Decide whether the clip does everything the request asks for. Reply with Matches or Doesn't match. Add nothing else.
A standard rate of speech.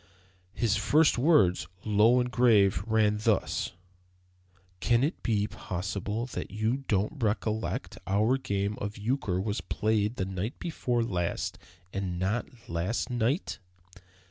Doesn't match